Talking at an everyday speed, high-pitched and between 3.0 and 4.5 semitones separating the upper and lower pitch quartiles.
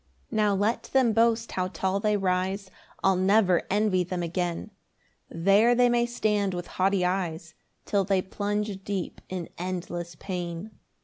No: average, 150 wpm; high, 195 Hz; narrow, 2.6 semitones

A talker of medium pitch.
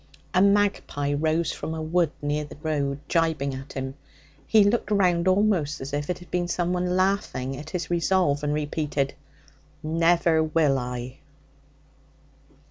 Yes: medium, 160 Hz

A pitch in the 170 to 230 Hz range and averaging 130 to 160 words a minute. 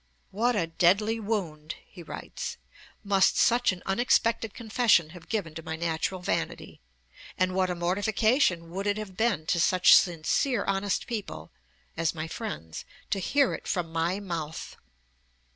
Yes: medium, 185 Hz; average, 150 wpm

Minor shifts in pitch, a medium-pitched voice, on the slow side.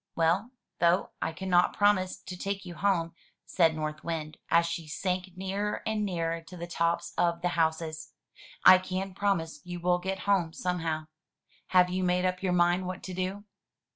No: narrow, 2.0 semitones; medium, 180 Hz; average, 180 wpm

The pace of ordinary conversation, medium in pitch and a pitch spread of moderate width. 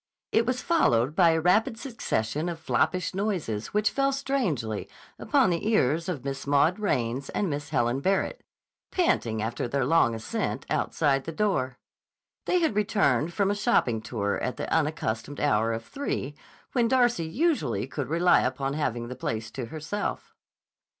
No: average, 160 wpm; medium, 155 Hz; wide, 8.8 semitones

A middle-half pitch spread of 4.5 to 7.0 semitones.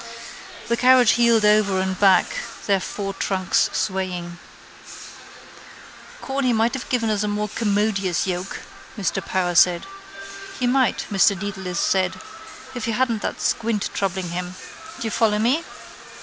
No: average, 3.5 semitones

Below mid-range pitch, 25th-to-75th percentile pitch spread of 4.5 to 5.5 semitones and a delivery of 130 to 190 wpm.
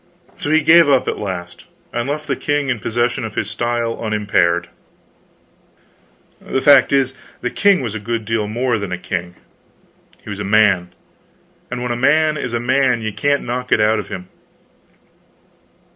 No: low, 120 Hz; average, 4.0 semitones; average, 175 wpm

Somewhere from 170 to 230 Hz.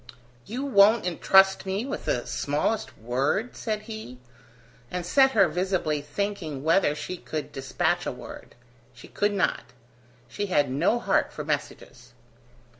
Yes: high, 190 Hz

